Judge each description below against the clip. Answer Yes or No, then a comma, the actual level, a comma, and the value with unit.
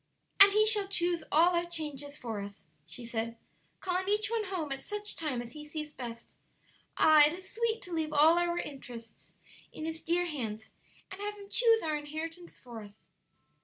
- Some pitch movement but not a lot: No, wide, 5.8 semitones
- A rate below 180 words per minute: No, average, 190 wpm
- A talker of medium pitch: No, very high, 320 Hz